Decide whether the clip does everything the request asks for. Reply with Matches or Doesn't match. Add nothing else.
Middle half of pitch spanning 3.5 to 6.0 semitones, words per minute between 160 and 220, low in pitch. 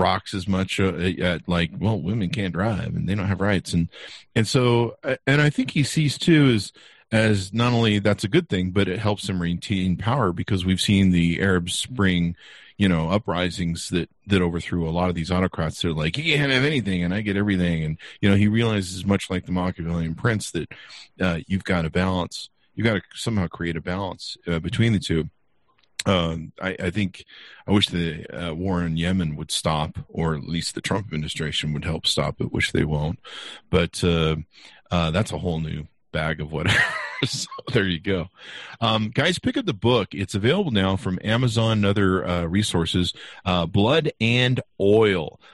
Matches